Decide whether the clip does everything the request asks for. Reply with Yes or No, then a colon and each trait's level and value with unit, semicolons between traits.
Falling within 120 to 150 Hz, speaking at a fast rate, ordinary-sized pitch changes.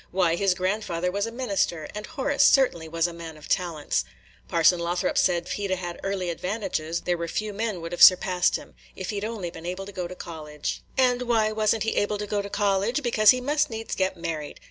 No: high, 190 Hz; fast, 235 wpm; average, 4.0 semitones